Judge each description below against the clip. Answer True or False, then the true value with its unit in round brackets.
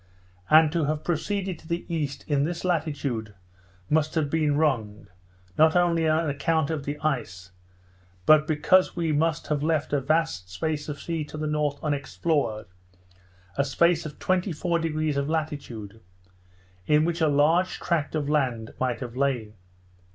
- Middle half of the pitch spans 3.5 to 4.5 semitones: False (2.6 semitones)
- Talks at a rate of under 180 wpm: True (155 wpm)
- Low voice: False (150 Hz)